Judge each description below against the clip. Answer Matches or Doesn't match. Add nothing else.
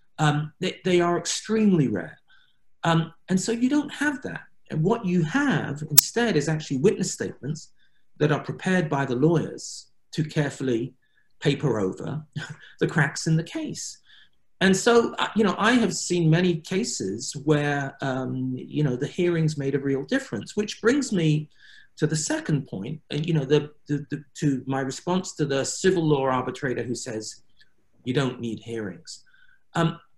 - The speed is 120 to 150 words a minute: Doesn't match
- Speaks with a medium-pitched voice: Matches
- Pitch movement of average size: Matches